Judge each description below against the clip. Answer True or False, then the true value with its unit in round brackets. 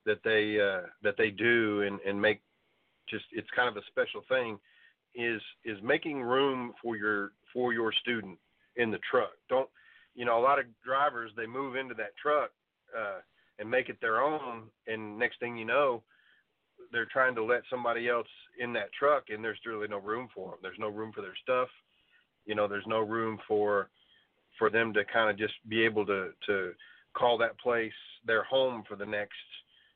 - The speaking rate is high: False (195 wpm)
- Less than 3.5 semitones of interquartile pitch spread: True (2.9 semitones)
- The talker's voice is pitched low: True (115 Hz)